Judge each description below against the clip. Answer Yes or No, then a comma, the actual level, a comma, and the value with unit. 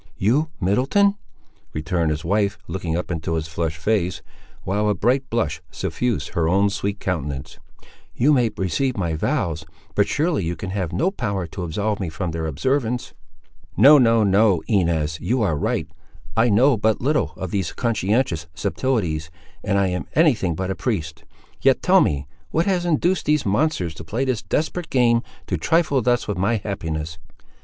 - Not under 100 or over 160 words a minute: No, average, 170 wpm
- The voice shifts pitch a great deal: Yes, wide, 6.7 semitones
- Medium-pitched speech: No, low, 100 Hz